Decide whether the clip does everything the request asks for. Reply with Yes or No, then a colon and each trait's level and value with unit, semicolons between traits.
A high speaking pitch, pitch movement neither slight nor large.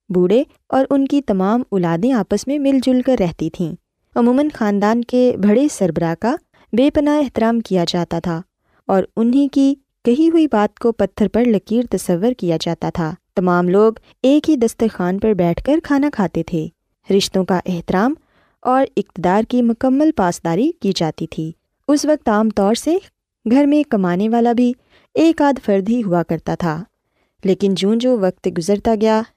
No: high, 220 Hz; wide, 5.8 semitones